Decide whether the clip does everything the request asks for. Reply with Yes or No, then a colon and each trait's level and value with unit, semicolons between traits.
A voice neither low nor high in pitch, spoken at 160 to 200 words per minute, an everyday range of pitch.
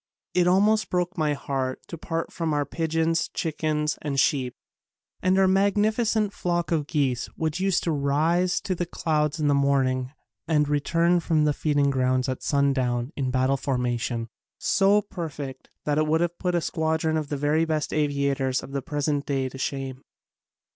Yes: medium, 150 Hz; average, 170 wpm; average, 3.7 semitones